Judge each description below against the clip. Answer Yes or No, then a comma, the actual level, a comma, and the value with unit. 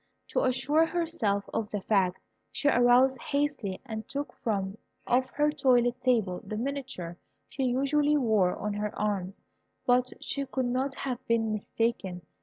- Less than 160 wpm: Yes, average, 150 wpm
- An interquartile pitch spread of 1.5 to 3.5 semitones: No, average, 4.5 semitones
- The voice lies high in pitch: Yes, high, 245 Hz